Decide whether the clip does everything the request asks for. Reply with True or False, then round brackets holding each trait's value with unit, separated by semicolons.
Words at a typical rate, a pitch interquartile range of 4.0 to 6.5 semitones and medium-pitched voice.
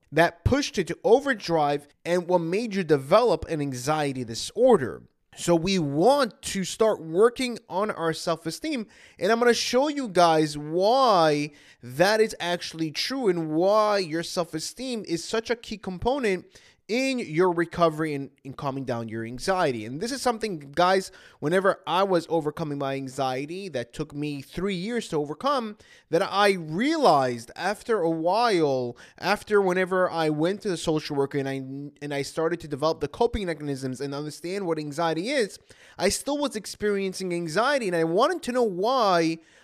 True (170 wpm; 5.5 semitones; 170 Hz)